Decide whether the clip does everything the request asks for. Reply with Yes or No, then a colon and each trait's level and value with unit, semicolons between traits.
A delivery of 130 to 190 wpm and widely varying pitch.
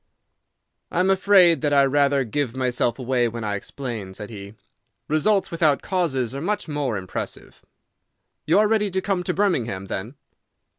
Yes: average, 160 wpm; wide, 7.2 semitones